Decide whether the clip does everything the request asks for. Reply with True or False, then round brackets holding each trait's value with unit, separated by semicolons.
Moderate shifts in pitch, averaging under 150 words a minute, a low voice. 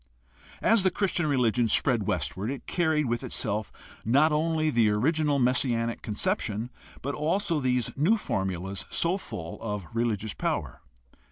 False (6.3 semitones; 140 wpm; 125 Hz)